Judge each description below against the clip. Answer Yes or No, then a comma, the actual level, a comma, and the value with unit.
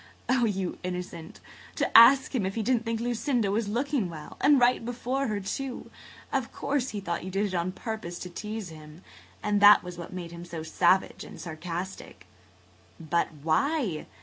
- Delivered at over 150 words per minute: Yes, average, 175 wpm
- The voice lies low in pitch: No, high, 200 Hz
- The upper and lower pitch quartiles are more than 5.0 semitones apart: Yes, wide, 5.6 semitones